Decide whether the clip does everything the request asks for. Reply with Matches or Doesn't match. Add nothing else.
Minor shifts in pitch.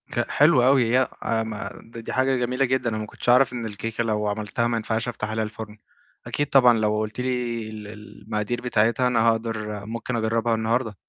Matches